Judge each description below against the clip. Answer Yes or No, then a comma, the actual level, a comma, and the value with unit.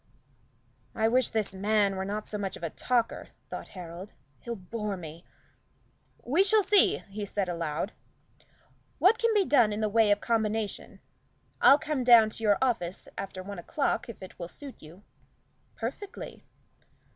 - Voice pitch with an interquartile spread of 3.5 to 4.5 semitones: Yes, average, 4.1 semitones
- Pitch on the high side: Yes, high, 210 Hz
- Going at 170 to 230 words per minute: No, average, 160 wpm